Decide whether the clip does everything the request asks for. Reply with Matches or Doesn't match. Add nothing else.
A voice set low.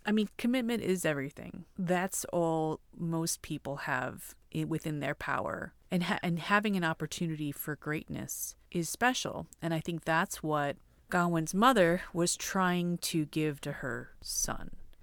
Doesn't match